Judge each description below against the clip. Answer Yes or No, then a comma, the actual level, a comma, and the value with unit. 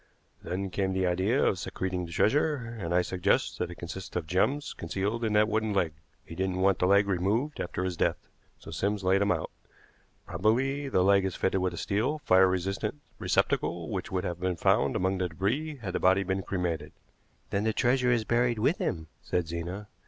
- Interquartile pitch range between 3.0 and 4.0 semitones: Yes, average, 3.3 semitones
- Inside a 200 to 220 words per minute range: Yes, fast, 205 wpm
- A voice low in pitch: Yes, very low, 95 Hz